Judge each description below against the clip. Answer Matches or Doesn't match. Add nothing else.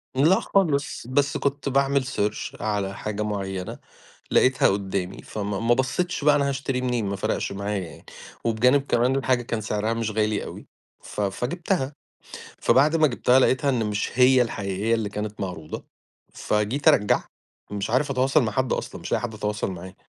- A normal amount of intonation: Matches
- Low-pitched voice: Matches